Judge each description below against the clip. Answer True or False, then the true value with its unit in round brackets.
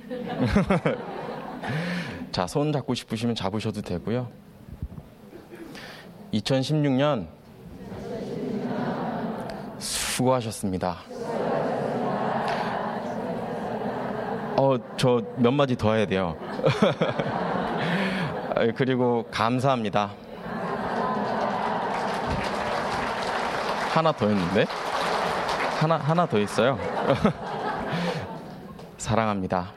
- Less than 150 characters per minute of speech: True (120 characters per minute)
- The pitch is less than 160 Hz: True (135 Hz)